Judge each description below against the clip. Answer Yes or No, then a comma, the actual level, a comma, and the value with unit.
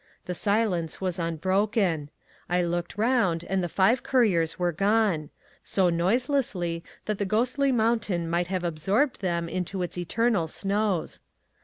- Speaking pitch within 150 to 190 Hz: Yes, medium, 185 Hz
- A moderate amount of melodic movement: Yes, average, 4.1 semitones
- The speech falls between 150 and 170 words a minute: No, average, 140 wpm